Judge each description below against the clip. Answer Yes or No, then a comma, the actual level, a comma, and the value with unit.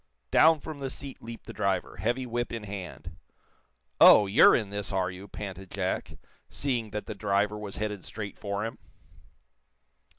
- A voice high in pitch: No, low, 105 Hz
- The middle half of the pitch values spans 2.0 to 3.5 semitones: Yes, average, 2.9 semitones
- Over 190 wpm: No, average, 165 wpm